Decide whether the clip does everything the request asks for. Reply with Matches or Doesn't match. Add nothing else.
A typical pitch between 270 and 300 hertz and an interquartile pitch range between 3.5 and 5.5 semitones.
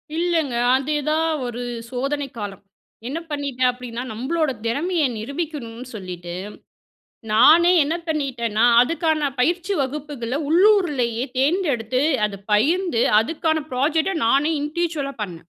Matches